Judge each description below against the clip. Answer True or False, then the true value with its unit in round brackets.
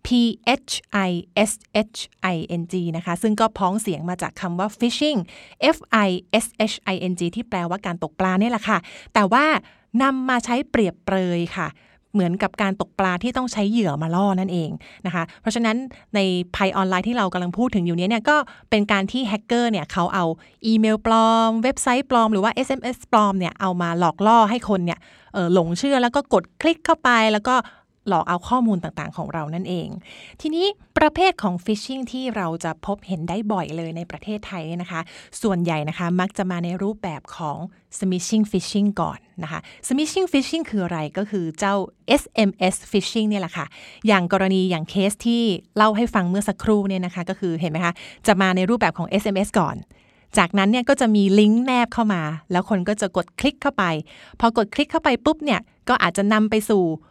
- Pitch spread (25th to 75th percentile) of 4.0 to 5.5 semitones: True (4.3 semitones)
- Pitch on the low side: False (205 Hz)